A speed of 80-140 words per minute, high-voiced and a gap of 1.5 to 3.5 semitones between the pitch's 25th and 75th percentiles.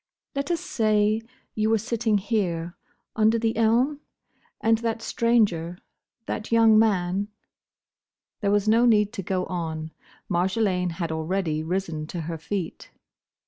No: slow, 135 wpm; high, 205 Hz; average, 4.2 semitones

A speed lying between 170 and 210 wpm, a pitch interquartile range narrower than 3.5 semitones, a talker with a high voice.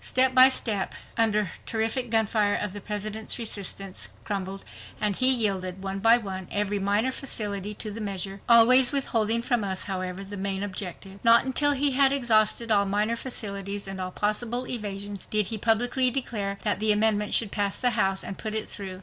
Yes: average, 180 wpm; average, 2.9 semitones; high, 210 Hz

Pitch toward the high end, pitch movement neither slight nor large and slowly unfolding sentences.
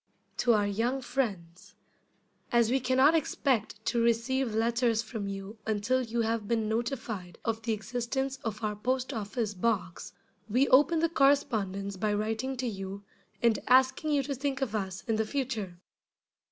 No: high, 230 Hz; average, 3.8 semitones; average, 165 wpm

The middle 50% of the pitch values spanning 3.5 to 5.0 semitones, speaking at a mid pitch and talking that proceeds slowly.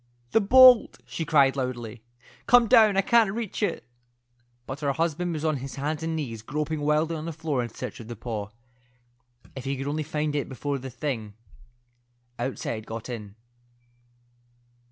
No: average, 4.6 semitones; medium, 145 Hz; average, 170 wpm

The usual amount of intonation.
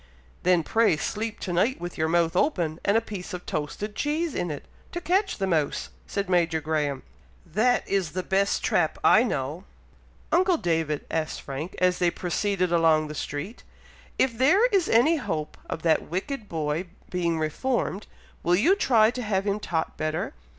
No: wide, 5.9 semitones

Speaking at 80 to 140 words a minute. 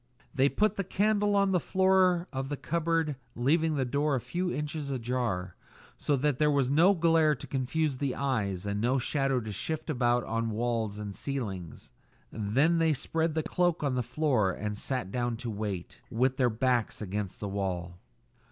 No: average, 180 wpm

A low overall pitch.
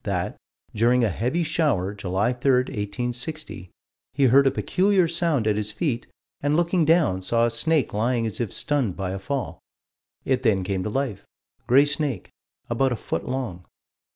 Yes: low, 125 Hz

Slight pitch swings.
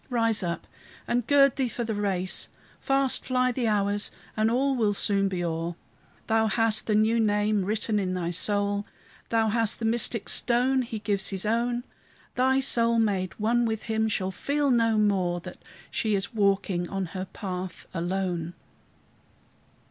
No: average, 3.2 semitones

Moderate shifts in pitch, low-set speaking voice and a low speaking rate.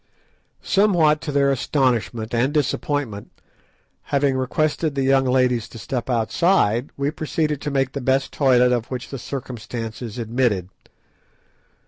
Yes: average, 3.2 semitones; low, 130 Hz; slow, 130 wpm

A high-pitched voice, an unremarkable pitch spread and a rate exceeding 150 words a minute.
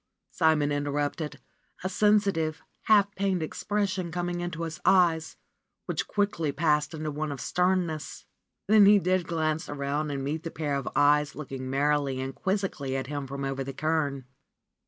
No: medium, 155 Hz; average, 3.8 semitones; average, 160 wpm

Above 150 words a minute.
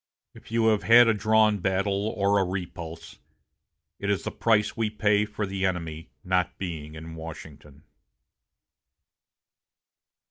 No: slow, 135 wpm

